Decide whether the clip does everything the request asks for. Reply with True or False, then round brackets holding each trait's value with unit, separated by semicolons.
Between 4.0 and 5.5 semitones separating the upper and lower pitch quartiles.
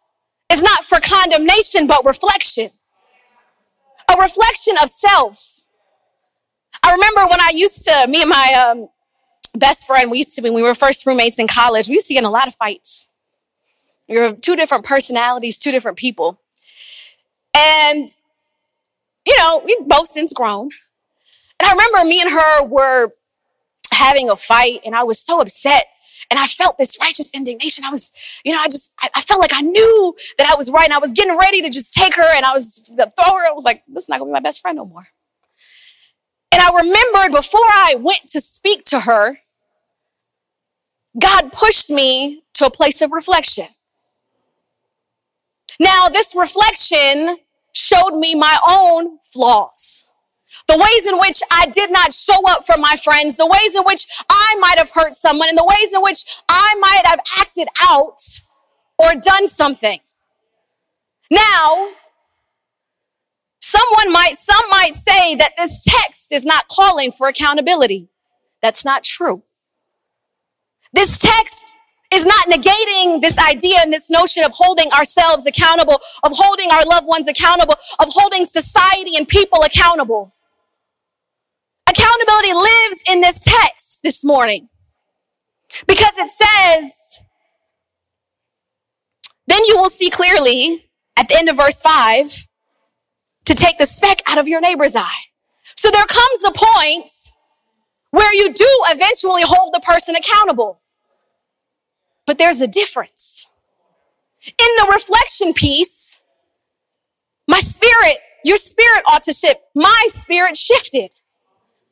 True (5.1 semitones)